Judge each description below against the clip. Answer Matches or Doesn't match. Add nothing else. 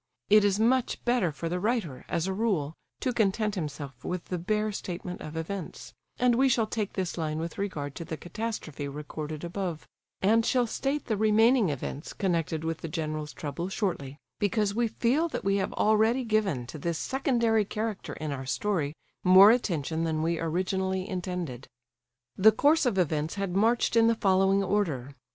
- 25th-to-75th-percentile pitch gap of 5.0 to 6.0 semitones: Matches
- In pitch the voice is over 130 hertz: Matches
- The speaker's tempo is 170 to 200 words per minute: Matches